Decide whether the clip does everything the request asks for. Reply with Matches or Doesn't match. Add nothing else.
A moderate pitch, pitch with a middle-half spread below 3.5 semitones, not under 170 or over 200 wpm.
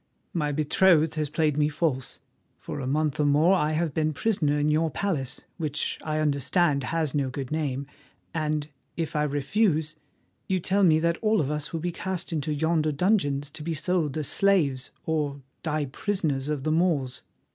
Matches